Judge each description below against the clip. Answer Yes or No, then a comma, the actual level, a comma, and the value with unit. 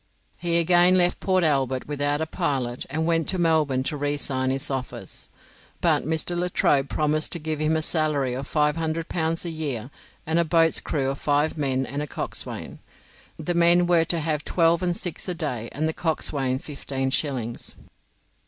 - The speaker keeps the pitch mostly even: No, average, 3.2 semitones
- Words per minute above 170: Yes, average, 180 wpm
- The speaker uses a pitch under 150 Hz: No, medium, 155 Hz